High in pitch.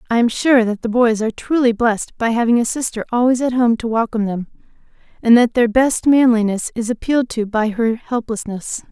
Yes: high, 235 Hz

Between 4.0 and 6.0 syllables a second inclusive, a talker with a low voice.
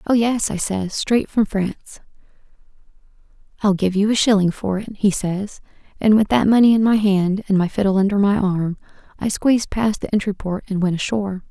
No: 5.4 syllables/s; high, 200 Hz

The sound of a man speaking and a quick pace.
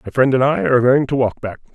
Yes: male; fast, 310 wpm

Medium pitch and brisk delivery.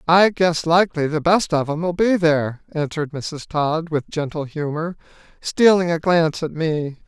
No: medium, 160 Hz; average, 170 wpm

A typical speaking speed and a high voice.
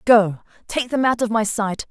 No: fast, 220 wpm; high, 225 Hz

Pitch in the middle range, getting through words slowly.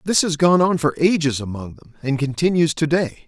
No: medium, 155 Hz; average, 200 wpm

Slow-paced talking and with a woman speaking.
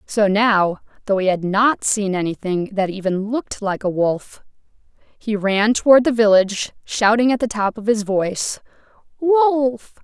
No: average, 160 wpm; female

